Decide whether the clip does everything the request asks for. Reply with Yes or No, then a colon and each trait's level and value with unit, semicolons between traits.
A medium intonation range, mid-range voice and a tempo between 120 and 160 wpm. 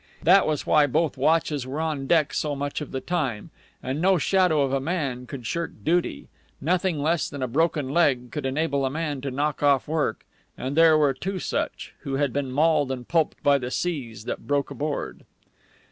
No: average, 3.3 semitones; medium, 145 Hz; average, 200 wpm